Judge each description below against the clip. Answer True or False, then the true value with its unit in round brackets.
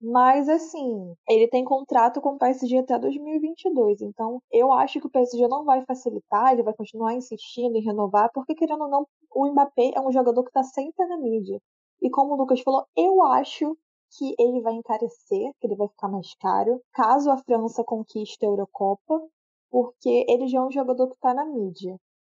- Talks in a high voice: True (255 Hz)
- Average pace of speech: False (195 wpm)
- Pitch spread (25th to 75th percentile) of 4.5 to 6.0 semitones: False (3.6 semitones)